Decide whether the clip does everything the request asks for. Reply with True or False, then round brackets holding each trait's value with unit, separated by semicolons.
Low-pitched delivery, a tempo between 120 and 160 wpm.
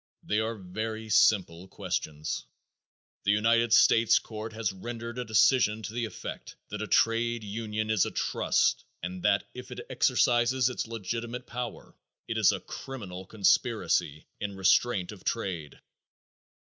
True (110 Hz; 145 wpm)